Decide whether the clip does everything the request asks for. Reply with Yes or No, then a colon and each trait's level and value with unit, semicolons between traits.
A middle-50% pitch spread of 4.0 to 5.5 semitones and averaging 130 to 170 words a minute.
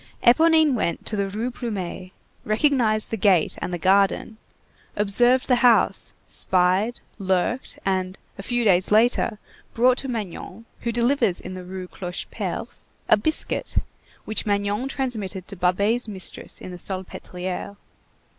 Yes: average, 4.4 semitones; slow, 135 wpm